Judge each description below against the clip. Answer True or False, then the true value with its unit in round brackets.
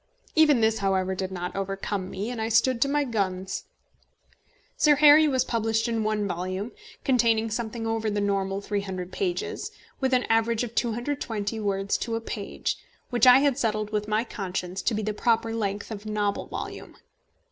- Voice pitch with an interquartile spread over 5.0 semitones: False (3.3 semitones)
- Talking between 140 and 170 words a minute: False (180 wpm)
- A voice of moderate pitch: False (220 Hz)